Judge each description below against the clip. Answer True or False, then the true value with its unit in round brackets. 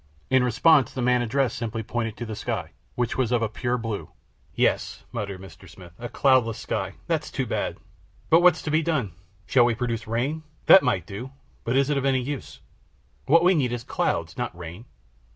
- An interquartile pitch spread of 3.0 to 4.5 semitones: True (3.5 semitones)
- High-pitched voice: False (120 Hz)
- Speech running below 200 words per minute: False (205 wpm)